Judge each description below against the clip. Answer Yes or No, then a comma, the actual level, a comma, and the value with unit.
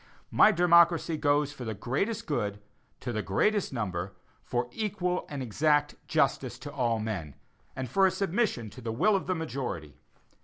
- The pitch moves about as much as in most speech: No, wide, 7.9 semitones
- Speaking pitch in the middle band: Yes, medium, 145 Hz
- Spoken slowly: No, average, 165 wpm